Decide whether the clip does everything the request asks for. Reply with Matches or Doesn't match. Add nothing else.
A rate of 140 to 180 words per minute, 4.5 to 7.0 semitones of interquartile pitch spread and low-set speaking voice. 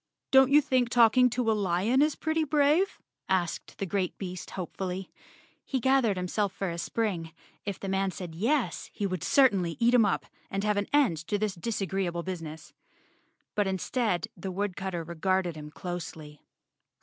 Doesn't match